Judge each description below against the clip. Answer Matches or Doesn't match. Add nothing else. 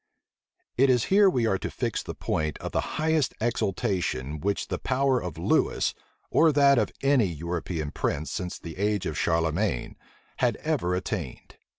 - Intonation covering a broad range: Matches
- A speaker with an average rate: Matches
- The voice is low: Matches